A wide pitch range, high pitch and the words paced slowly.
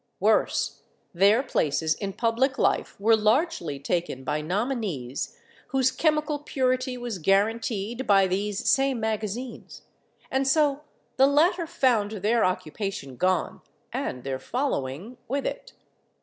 Yes: wide, 6.0 semitones; high, 220 Hz; slow, 120 wpm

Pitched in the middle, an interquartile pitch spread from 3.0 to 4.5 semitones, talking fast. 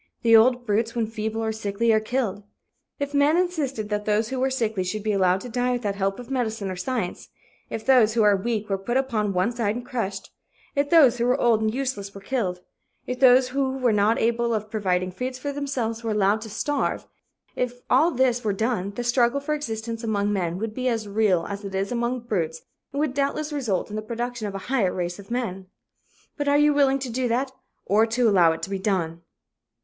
No: high, 225 Hz; average, 3.8 semitones; fast, 225 wpm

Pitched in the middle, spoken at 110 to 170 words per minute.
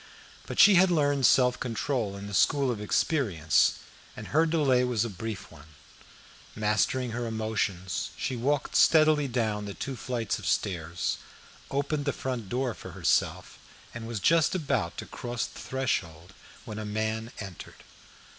No: low, 120 Hz; average, 155 wpm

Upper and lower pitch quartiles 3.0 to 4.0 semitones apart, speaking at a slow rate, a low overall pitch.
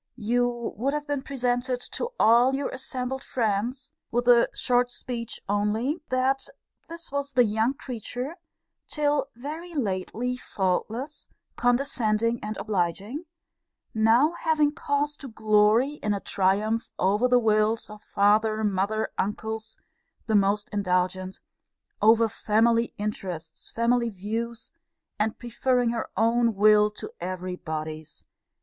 No: average, 3.5 semitones; slow, 125 wpm; high, 230 Hz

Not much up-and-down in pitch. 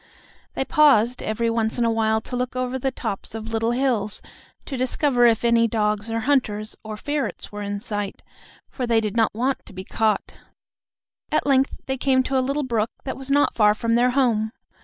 No: average, 3.1 semitones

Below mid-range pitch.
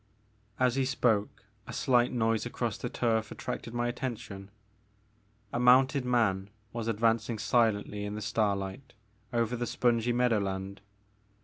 Yes: low, 115 Hz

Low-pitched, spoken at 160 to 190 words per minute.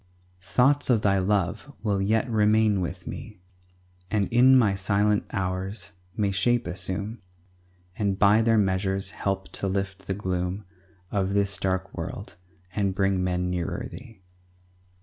No: low, 100 Hz; average, 140 wpm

